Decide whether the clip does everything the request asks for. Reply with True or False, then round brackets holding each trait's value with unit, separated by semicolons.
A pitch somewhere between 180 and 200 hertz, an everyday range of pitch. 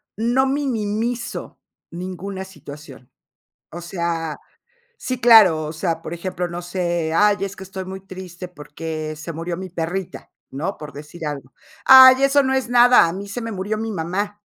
True (185 Hz; 4.4 semitones)